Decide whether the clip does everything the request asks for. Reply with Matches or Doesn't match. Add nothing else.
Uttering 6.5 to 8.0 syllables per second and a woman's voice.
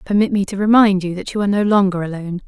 Matches